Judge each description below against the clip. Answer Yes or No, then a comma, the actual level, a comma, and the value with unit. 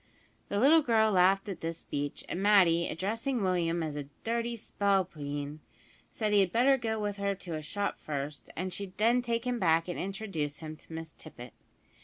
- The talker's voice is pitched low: No, high, 190 Hz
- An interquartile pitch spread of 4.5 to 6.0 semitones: Yes, average, 5.2 semitones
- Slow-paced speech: No, average, 190 wpm